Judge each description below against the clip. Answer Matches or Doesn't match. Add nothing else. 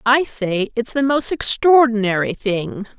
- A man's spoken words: Doesn't match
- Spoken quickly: Doesn't match